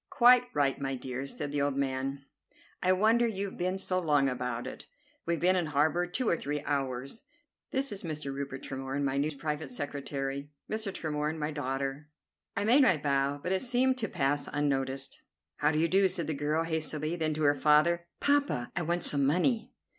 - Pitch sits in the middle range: Yes, medium, 150 Hz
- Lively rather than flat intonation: No, average, 4.6 semitones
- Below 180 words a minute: No, average, 190 wpm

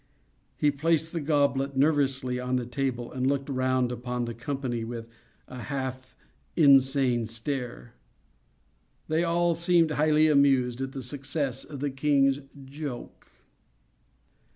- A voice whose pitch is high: No, low, 135 Hz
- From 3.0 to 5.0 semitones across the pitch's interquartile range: No, narrow, 2.6 semitones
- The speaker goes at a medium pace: No, slow, 130 wpm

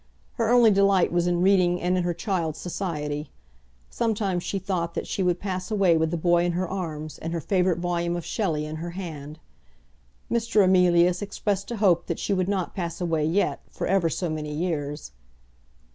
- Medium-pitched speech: Yes, medium, 175 Hz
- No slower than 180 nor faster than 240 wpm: Yes, average, 190 wpm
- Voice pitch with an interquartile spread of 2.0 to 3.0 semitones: Yes, average, 2.7 semitones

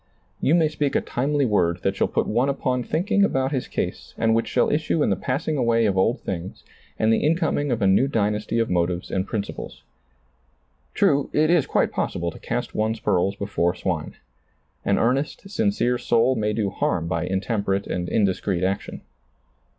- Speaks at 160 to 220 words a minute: Yes, average, 190 wpm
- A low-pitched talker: Yes, low, 115 Hz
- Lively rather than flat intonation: Yes, wide, 6.2 semitones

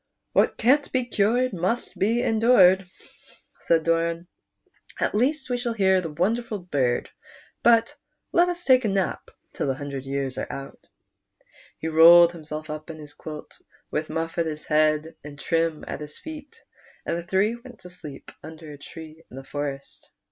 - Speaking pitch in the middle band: Yes, medium, 170 Hz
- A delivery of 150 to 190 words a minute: Yes, average, 175 wpm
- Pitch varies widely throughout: Yes, wide, 6.9 semitones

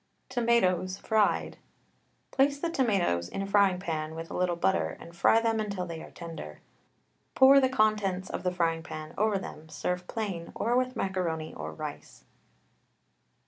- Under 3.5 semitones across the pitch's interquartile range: No, average, 5.0 semitones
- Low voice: No, medium, 185 Hz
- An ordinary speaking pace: Yes, average, 160 wpm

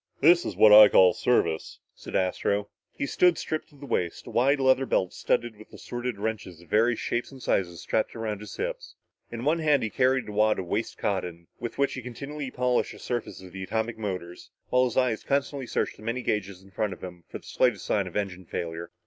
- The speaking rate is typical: No, fast, 225 wpm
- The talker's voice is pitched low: Yes, low, 110 Hz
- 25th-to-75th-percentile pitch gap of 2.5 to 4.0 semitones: No, average, 5.2 semitones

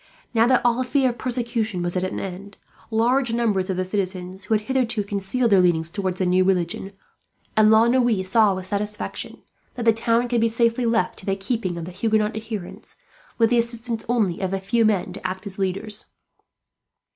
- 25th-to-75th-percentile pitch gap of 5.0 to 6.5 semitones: No, average, 3.7 semitones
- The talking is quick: Yes, fast, 210 wpm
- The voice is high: Yes, high, 210 Hz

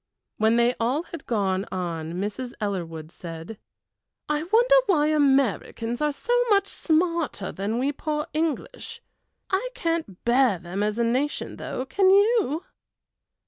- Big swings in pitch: Yes, wide, 8.2 semitones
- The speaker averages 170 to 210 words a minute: No, average, 140 wpm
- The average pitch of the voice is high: Yes, very high, 260 Hz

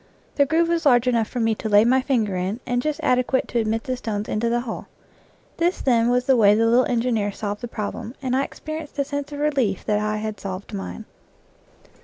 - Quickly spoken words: Yes, fast, 225 wpm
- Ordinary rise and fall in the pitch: Yes, average, 3.7 semitones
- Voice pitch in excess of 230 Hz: Yes, high, 240 Hz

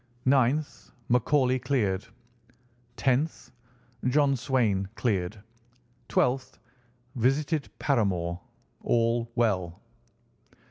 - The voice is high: No, low, 125 Hz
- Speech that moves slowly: Yes, slow, 65 wpm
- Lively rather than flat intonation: No, average, 4.7 semitones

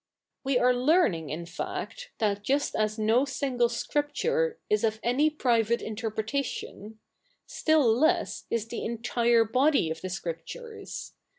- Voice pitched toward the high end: Yes, high, 240 Hz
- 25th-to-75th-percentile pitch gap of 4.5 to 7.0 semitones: Yes, average, 5.1 semitones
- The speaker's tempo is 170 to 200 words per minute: No, average, 140 wpm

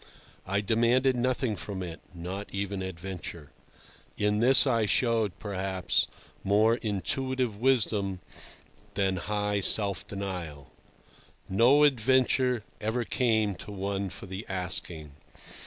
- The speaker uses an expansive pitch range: No, average, 3.8 semitones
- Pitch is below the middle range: Yes, low, 100 Hz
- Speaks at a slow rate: Yes, slow, 105 wpm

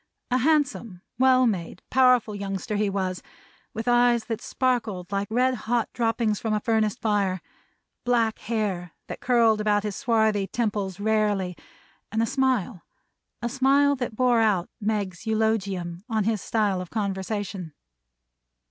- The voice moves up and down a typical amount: Yes, average, 3.2 semitones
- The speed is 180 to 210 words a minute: No, average, 145 wpm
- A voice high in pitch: Yes, high, 220 Hz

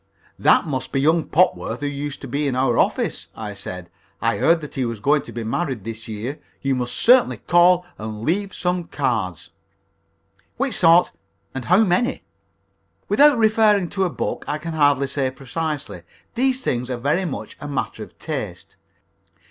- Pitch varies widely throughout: Yes, wide, 5.8 semitones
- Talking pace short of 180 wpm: Yes, average, 170 wpm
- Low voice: No, medium, 145 Hz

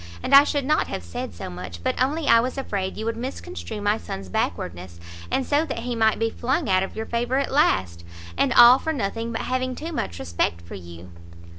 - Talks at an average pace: No, fast, 225 wpm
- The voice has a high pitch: Yes, high, 225 Hz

